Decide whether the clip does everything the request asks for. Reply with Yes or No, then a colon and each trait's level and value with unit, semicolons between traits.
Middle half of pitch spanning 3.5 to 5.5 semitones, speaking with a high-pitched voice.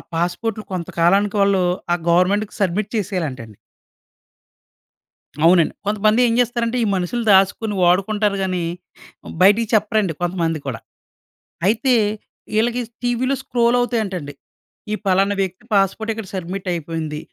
Yes: average, 3.8 semitones; high, 195 Hz